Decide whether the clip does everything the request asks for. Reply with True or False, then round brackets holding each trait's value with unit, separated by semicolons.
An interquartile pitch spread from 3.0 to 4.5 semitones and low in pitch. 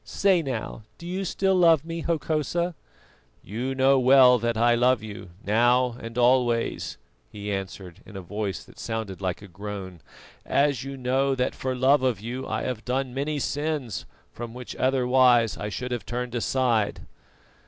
True (3.5 semitones; 125 Hz)